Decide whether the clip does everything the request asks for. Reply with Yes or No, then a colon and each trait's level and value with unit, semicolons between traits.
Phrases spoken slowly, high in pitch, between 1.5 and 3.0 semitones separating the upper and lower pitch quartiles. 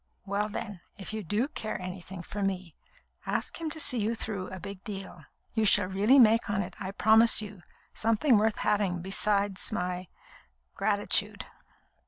No: average, 165 wpm; high, 205 Hz; narrow, 2.6 semitones